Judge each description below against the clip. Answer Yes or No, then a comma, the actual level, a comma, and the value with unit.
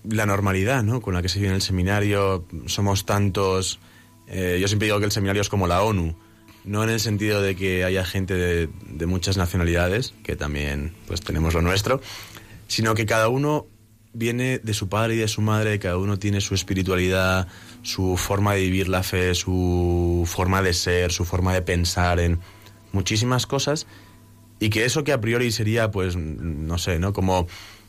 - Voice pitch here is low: Yes, low, 100 Hz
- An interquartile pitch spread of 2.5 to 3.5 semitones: Yes, average, 3.1 semitones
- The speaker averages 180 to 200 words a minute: Yes, average, 185 wpm